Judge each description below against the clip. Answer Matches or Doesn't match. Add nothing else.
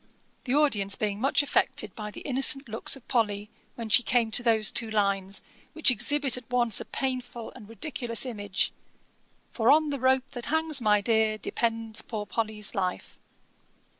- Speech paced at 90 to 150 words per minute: Doesn't match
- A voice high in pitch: Matches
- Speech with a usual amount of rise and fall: Matches